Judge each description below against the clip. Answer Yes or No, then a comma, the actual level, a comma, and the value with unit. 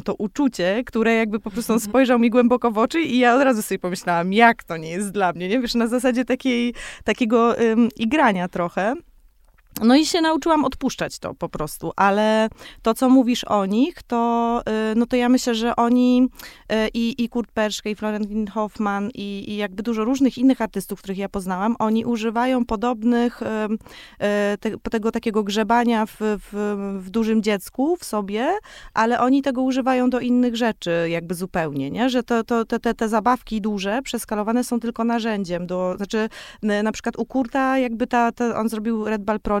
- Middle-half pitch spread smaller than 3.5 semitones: Yes, average, 2.8 semitones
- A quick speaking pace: Yes, fast, 185 wpm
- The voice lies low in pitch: No, high, 230 Hz